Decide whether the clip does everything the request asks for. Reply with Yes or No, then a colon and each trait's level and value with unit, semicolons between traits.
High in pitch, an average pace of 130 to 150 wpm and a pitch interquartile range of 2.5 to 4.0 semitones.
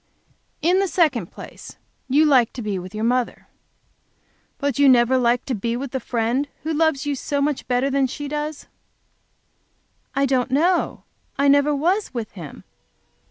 No: very high, 275 Hz; average, 165 wpm; average, 3.4 semitones